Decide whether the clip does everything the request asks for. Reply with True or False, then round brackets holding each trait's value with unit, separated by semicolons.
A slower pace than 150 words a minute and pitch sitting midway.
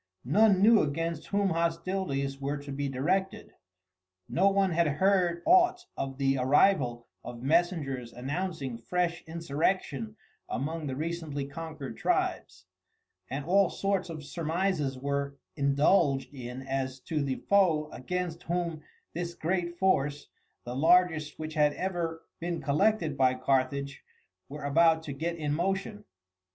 True (135 wpm; 155 Hz)